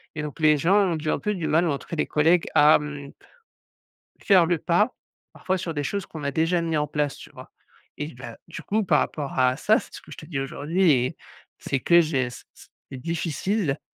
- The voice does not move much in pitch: No, average, 3.3 semitones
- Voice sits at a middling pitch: Yes, medium, 155 Hz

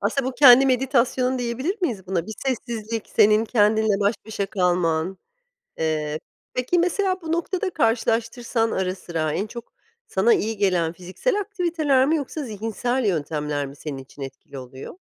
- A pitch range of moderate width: No, wide, 6.3 semitones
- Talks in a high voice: Yes, high, 220 Hz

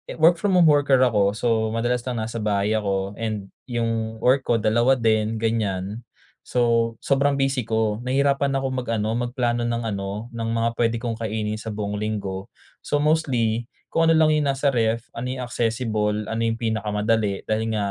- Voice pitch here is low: Yes, low, 115 Hz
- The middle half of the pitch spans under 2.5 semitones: No, average, 2.8 semitones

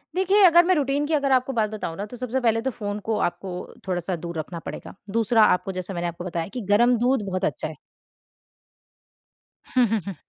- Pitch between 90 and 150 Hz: No, high, 220 Hz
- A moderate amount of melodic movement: No, wide, 5.9 semitones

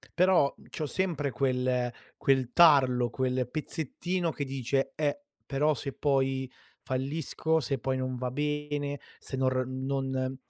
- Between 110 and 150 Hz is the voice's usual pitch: Yes, low, 135 Hz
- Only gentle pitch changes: Yes, narrow, 2.3 semitones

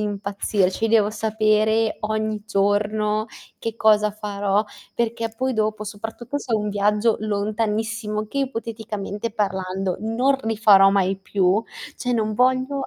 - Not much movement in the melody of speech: Yes, narrow, 1.6 semitones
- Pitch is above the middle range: Yes, high, 215 Hz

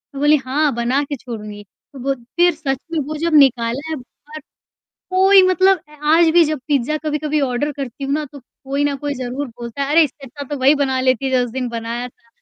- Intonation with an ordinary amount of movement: Yes, average, 3.3 semitones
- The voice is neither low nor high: No, very high, 280 Hz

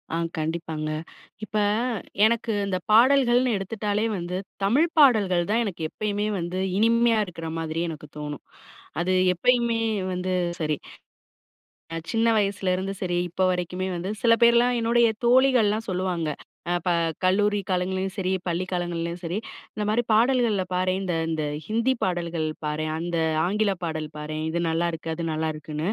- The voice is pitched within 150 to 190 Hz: Yes, medium, 185 Hz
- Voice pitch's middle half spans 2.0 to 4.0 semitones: No, average, 4.6 semitones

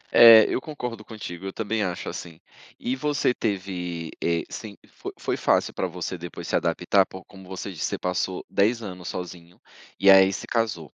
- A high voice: No, very low, 95 Hz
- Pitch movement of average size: Yes, average, 3.9 semitones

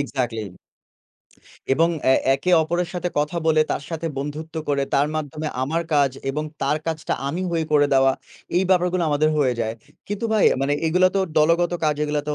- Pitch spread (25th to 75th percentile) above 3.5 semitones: No, average, 3.1 semitones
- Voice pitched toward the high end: No, medium, 155 Hz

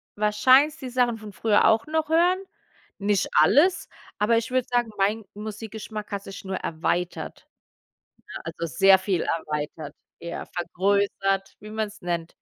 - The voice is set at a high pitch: Yes, high, 210 Hz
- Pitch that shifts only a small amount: No, average, 3.3 semitones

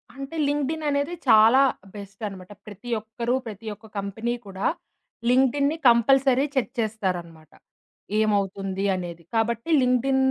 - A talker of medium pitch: No, high, 225 Hz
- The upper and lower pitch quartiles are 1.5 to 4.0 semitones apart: No, average, 5.0 semitones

